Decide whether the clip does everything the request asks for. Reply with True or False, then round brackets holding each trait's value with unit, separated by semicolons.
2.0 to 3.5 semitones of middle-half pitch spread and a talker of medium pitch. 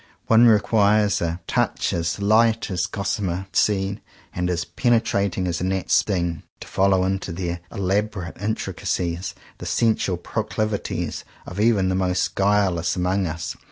False (2.8 semitones; 95 Hz)